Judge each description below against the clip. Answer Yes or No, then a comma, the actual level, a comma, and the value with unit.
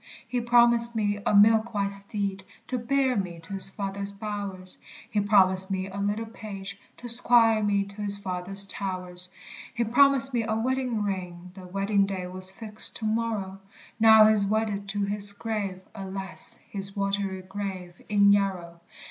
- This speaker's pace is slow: No, average, 165 wpm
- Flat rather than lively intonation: Yes, narrow, 2.3 semitones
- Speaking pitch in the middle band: No, high, 200 Hz